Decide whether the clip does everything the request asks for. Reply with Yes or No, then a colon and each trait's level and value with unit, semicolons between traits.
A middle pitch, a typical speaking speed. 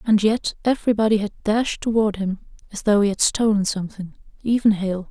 No: high, 210 Hz; average, 165 wpm